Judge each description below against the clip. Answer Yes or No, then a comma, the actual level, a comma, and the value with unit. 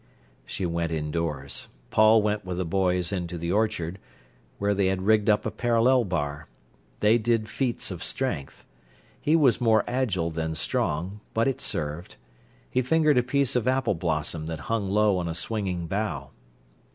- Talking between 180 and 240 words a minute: No, average, 165 wpm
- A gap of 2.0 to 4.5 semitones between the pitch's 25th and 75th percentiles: No, average, 5.3 semitones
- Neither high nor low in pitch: No, low, 100 Hz